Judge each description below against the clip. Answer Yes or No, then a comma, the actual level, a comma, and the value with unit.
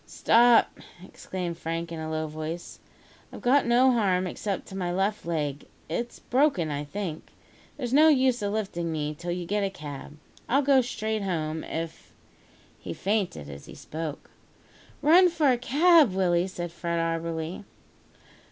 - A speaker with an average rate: Yes, average, 160 wpm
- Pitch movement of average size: No, wide, 6.5 semitones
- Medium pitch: Yes, medium, 180 Hz